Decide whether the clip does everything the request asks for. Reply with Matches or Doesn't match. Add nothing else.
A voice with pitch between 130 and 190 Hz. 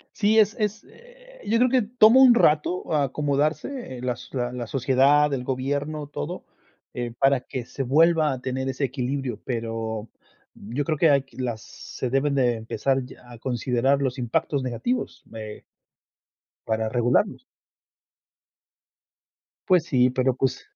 Matches